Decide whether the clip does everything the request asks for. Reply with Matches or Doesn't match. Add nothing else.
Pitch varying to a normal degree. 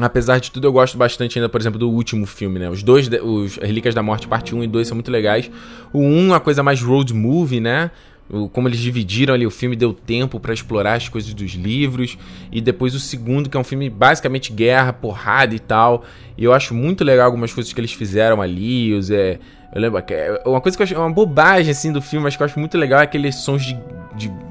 Matches